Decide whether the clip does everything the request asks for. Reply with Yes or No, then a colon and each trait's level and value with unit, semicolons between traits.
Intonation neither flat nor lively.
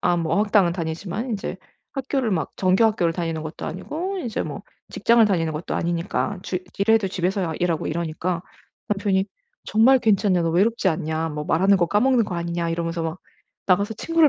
Yes: average, 4.3 semitones